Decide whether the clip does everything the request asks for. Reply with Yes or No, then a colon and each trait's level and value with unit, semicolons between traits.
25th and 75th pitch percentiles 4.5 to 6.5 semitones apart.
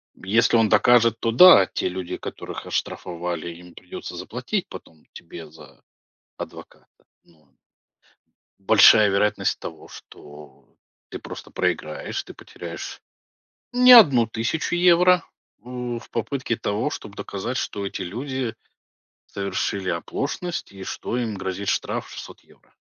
Yes: wide, 5.4 semitones